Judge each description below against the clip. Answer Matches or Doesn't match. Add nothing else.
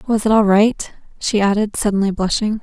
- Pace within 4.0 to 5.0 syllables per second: Doesn't match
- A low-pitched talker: Doesn't match